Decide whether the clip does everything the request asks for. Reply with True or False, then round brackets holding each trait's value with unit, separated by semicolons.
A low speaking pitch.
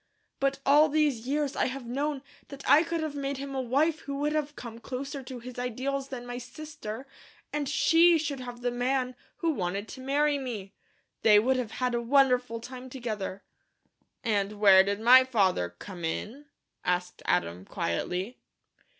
False (255 Hz)